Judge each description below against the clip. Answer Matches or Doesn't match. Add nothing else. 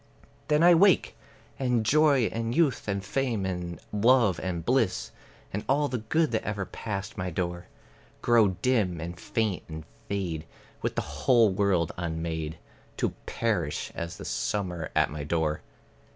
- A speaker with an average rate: Matches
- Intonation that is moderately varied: Doesn't match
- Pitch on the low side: Matches